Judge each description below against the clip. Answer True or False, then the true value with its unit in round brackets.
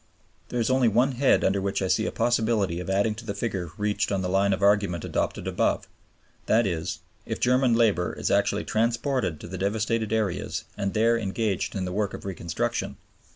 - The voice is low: True (105 Hz)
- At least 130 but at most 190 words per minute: False (200 wpm)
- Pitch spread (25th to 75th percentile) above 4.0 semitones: False (3.2 semitones)